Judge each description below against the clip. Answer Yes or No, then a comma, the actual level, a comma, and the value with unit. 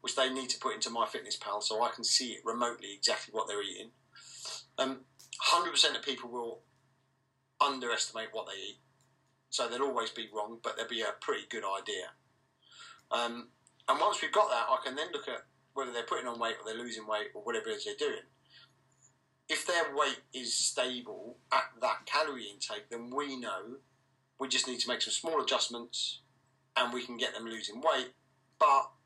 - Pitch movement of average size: No, narrow, 2.0 semitones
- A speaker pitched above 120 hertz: Yes, low, 130 Hz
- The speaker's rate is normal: Yes, average, 195 wpm